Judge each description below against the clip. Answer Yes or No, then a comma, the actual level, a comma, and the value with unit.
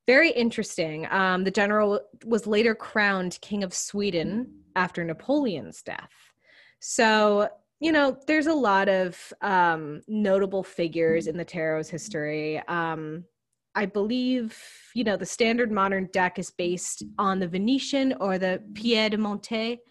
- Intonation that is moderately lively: Yes, average, 4.3 semitones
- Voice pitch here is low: No, high, 195 Hz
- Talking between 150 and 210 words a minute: No, average, 140 wpm